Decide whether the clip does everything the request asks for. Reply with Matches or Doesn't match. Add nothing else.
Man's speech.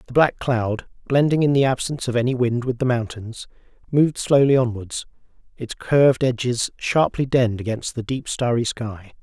Matches